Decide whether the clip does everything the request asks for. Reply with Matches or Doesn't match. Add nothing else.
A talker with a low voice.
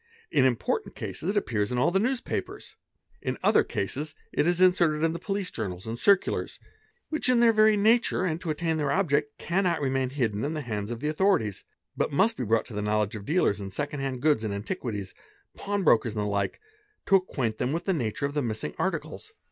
Doesn't match